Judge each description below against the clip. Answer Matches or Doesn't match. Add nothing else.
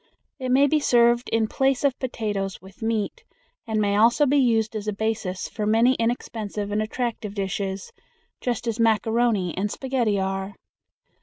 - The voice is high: Matches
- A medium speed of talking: Matches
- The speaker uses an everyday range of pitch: Matches